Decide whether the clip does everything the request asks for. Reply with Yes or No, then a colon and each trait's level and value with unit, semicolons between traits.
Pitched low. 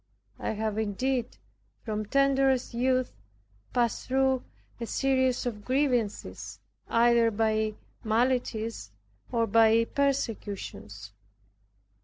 No: high, 230 Hz